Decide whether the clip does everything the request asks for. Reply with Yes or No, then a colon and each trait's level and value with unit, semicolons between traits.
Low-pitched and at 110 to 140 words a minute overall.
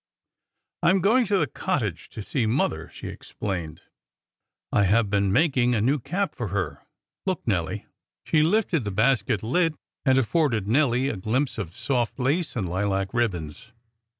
No: low, 120 Hz; average, 160 wpm